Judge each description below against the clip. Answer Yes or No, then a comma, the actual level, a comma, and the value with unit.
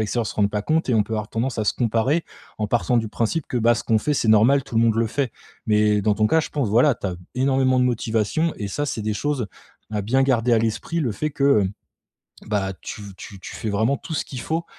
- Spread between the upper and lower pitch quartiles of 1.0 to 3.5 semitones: No, average, 4.0 semitones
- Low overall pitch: Yes, low, 115 Hz